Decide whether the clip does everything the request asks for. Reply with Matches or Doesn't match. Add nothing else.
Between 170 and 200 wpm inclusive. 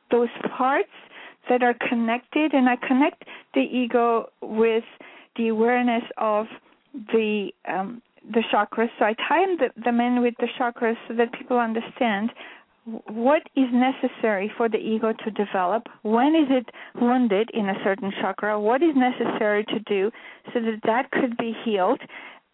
Doesn't match